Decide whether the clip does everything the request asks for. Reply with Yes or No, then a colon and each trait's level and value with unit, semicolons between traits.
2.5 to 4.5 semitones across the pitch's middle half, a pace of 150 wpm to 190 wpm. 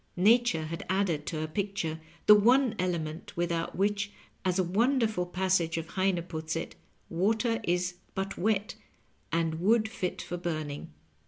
Yes: average, 3.8 semitones; average, 155 wpm